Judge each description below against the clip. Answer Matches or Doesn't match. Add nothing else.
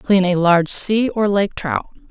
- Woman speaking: Matches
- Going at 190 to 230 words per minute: Matches